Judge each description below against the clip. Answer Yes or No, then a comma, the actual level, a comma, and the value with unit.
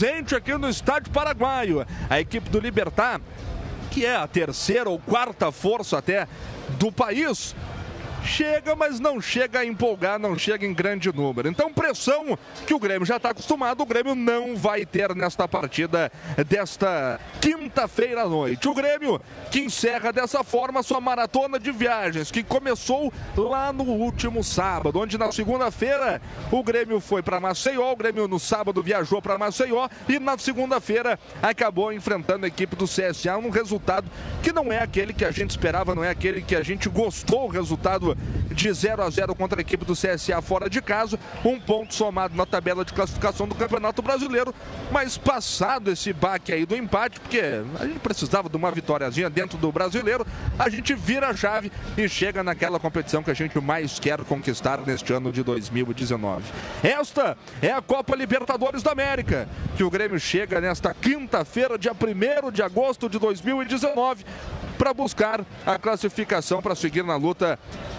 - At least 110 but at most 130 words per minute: No, average, 170 wpm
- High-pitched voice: Yes, high, 215 Hz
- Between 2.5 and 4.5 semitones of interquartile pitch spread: No, wide, 5.6 semitones